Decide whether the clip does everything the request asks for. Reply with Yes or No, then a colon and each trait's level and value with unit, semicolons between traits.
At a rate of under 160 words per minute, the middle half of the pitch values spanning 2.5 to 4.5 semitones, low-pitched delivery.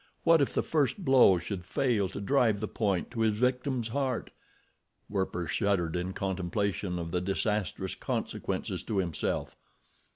No: average, 150 wpm; average, 5.3 semitones; low, 100 Hz